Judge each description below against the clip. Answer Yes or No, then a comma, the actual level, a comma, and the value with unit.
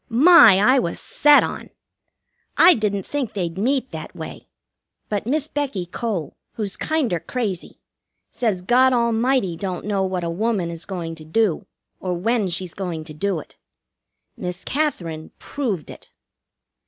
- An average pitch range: No, wide, 5.8 semitones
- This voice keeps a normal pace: Yes, average, 150 wpm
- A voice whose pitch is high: Yes, high, 200 Hz